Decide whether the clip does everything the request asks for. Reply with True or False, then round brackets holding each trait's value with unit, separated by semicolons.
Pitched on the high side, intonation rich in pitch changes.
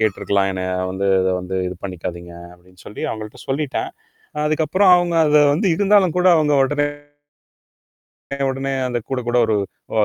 False (125 Hz; 8.5 semitones)